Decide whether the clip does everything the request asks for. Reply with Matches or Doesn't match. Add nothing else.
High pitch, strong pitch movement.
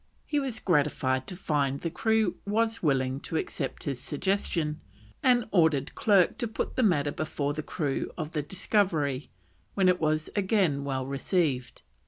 Doesn't match